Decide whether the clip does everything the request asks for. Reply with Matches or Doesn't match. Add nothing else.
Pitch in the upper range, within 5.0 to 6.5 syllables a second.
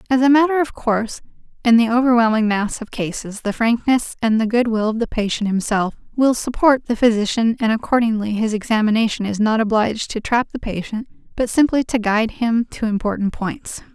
Matches